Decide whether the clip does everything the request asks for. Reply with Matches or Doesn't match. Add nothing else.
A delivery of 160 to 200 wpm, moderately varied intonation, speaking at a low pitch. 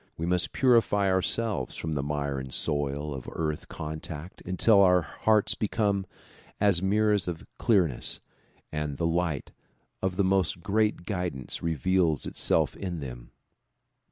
Doesn't match